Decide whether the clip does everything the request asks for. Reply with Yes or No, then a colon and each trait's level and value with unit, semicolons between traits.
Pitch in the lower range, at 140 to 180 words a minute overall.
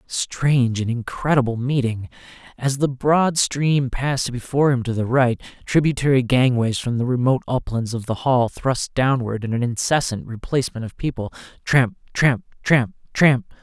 Yes: low, 125 Hz; average, 155 wpm